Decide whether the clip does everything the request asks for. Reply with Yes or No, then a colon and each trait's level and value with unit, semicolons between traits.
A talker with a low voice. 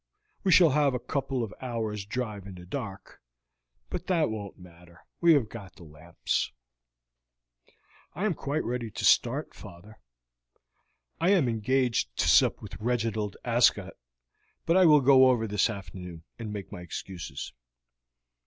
Yes: low, 115 Hz